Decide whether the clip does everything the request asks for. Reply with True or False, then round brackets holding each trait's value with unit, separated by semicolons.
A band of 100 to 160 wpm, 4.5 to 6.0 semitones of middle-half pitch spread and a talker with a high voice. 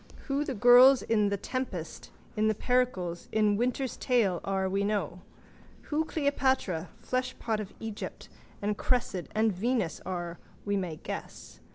True (140 wpm; 4.9 semitones; 215 Hz)